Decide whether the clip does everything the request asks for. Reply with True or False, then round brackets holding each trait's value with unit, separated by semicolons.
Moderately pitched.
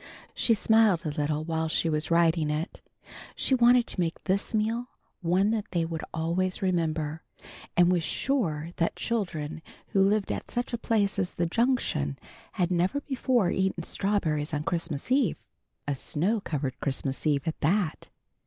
True (175 Hz)